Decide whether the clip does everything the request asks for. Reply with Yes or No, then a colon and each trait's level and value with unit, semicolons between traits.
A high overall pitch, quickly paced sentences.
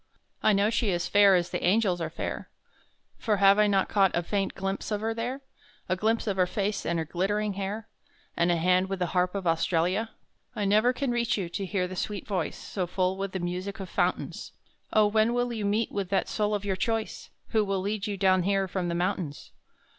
Yes: high, 195 Hz; fast, 225 wpm